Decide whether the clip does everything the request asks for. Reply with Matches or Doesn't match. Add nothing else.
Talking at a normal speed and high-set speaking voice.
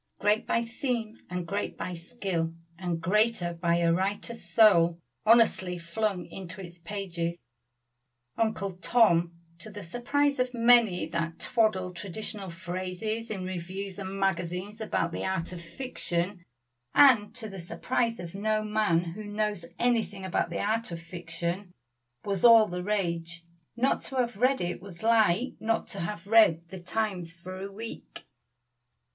Matches